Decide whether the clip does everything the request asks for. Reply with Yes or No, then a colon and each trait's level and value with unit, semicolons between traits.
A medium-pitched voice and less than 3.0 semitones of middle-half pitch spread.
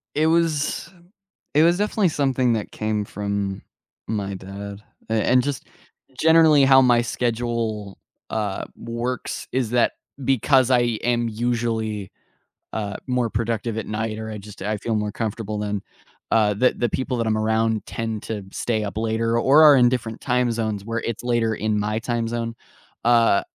No: low, 115 Hz; narrow, 2.6 semitones